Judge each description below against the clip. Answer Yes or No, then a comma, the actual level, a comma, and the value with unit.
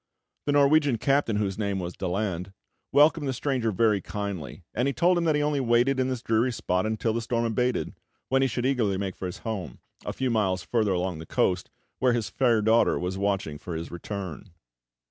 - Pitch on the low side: Yes, low, 110 Hz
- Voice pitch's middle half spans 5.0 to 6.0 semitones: Yes, average, 5.3 semitones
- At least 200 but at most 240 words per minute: Yes, fast, 205 wpm